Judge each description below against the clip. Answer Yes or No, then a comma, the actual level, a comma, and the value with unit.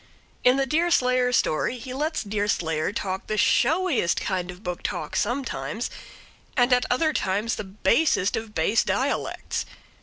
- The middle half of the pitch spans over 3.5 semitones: Yes, wide, 5.4 semitones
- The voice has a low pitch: No, high, 230 Hz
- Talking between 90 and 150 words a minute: Yes, average, 145 wpm